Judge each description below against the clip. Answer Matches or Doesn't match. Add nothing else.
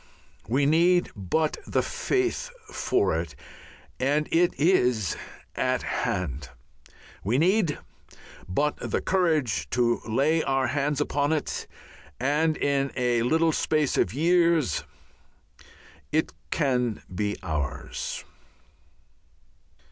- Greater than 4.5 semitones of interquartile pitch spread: Matches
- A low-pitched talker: Doesn't match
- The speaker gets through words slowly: Matches